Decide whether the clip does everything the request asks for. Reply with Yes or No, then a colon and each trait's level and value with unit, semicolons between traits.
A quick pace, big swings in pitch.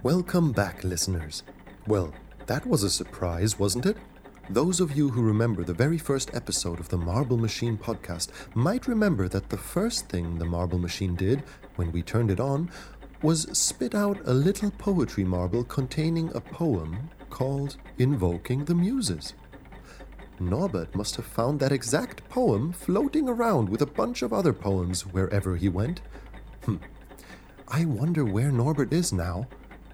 No: average, 155 wpm; wide, 8.8 semitones